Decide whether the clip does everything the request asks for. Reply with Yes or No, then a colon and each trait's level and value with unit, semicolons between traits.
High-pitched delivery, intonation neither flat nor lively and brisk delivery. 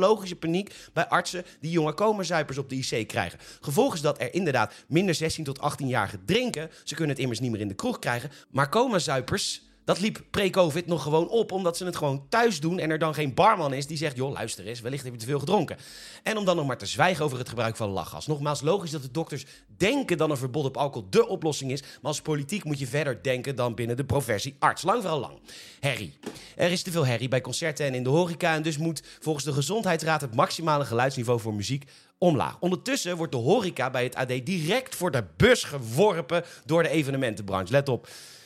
No: medium, 150 Hz; average, 5.0 semitones; fast, 225 wpm